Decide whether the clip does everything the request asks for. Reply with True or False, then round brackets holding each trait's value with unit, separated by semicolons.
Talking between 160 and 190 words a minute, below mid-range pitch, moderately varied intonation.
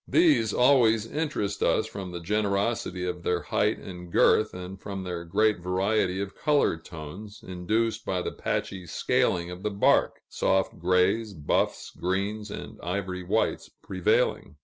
False (150 wpm; 95 Hz; 3.1 semitones)